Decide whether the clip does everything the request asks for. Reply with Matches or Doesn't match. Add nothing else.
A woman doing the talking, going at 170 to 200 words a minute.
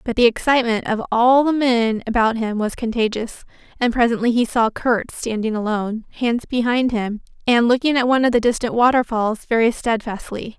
Matches